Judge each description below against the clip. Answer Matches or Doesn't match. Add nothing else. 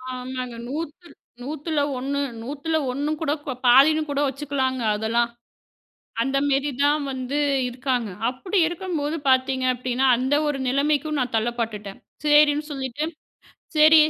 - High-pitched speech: Matches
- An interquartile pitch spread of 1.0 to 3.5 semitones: Matches